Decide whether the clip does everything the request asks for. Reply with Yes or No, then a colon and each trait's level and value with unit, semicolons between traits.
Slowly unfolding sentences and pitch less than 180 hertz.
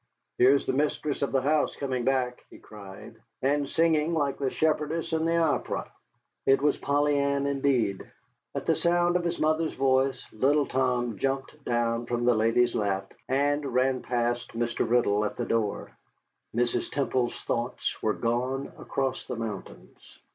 No: average, 160 wpm; low, 135 Hz